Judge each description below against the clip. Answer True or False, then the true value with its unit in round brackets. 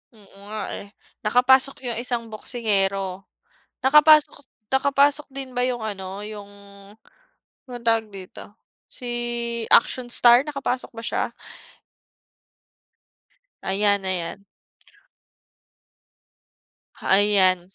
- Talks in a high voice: True (225 Hz)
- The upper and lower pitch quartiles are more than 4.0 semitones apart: True (4.5 semitones)